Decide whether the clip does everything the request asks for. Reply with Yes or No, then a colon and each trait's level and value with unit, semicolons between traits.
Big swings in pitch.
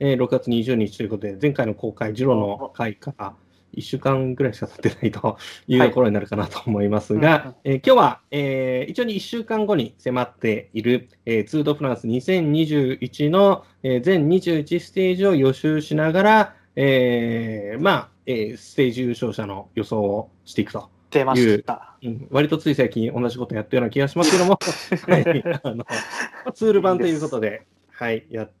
Yes: wide, 5.7 semitones